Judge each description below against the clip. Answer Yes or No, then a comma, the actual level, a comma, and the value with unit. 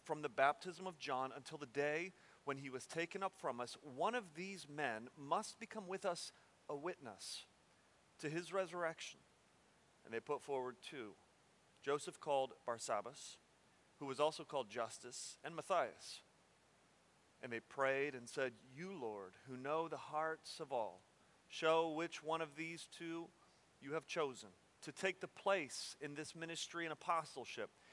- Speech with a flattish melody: No, average, 3.9 semitones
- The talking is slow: No, average, 160 wpm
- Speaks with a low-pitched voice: No, medium, 160 Hz